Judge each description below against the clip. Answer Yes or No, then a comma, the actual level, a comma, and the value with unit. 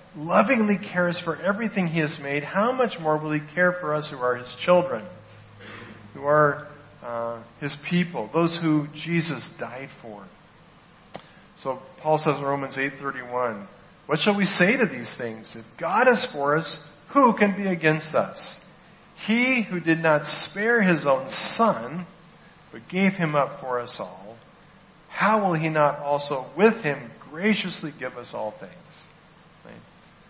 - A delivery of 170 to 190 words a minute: No, average, 160 wpm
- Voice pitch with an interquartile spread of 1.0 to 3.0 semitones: No, average, 4.3 semitones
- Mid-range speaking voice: Yes, medium, 155 Hz